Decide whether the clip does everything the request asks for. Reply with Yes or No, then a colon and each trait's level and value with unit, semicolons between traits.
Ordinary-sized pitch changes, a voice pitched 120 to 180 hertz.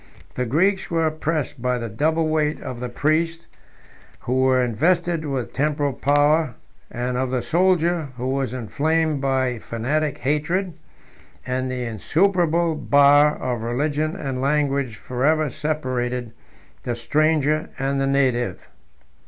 Yes: average, 3.6 semitones; medium, 140 Hz